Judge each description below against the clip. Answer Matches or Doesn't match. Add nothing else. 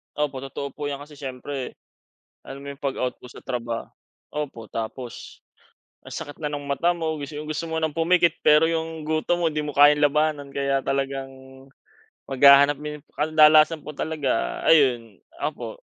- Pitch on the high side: Doesn't match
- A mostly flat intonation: Matches